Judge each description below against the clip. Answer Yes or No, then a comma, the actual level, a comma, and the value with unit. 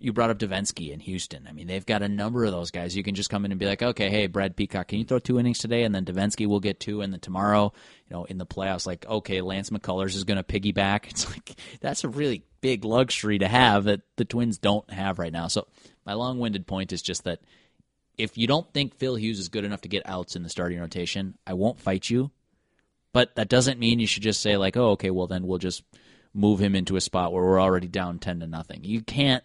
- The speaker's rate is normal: No, fast, 260 wpm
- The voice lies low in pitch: Yes, low, 100 Hz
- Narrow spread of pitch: No, average, 3.1 semitones